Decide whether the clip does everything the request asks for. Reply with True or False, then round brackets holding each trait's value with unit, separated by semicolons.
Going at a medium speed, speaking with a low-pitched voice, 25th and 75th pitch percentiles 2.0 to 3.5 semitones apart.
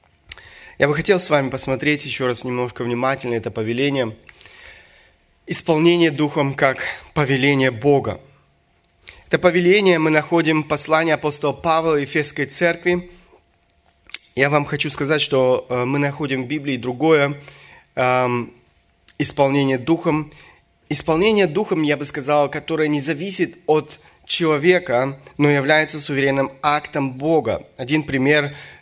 False (120 wpm; 145 Hz; 3.0 semitones)